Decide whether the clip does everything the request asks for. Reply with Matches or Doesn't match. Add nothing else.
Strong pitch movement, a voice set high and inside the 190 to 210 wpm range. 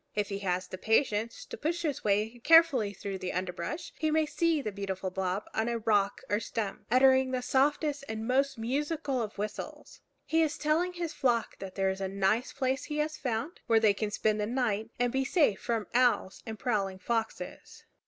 Matches